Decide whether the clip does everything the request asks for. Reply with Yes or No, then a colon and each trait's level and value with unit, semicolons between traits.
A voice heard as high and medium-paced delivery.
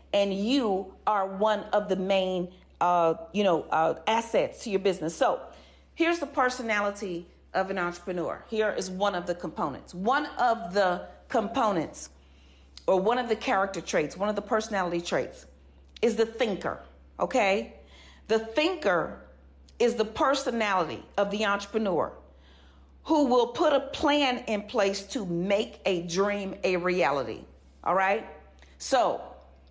Yes: high, 195 Hz; average, 145 wpm